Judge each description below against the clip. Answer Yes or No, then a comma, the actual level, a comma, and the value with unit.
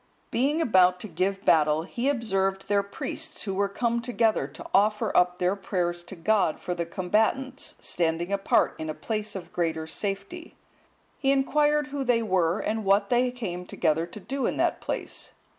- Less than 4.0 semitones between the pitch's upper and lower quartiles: No, average, 4.9 semitones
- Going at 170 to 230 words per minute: Yes, average, 175 wpm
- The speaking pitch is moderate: No, high, 200 Hz